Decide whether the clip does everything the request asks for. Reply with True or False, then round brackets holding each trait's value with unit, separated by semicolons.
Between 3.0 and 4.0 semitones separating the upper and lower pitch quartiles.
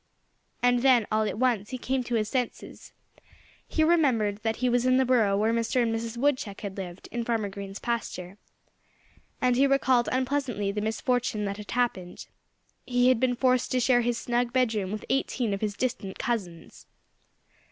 True (3.3 semitones)